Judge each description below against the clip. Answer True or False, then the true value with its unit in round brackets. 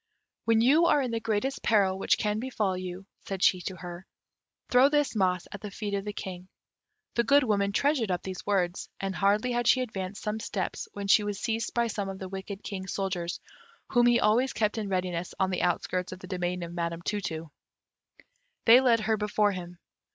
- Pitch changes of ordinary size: True (3.5 semitones)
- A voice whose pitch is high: True (200 Hz)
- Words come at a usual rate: False (210 wpm)